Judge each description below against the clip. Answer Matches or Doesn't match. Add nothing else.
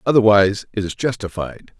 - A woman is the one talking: Doesn't match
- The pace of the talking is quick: Doesn't match